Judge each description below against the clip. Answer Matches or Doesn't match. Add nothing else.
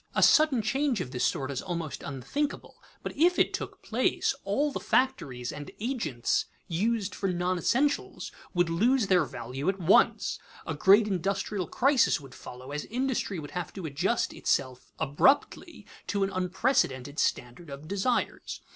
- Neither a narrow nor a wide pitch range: Doesn't match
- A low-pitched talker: Doesn't match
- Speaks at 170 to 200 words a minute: Doesn't match